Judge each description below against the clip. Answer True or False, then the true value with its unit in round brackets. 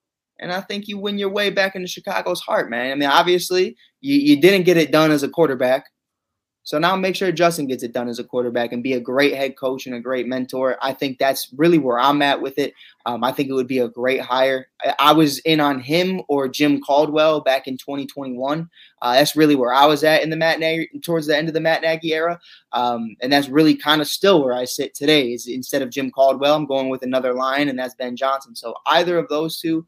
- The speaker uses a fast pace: True (250 wpm)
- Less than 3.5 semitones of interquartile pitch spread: False (3.9 semitones)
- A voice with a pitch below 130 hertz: False (140 Hz)